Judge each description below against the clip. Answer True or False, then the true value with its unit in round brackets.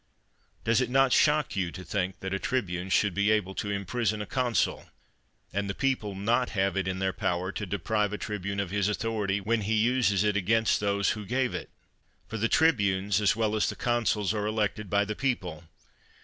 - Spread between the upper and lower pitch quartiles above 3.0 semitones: False (2.6 semitones)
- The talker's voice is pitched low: True (105 Hz)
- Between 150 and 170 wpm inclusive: False (205 wpm)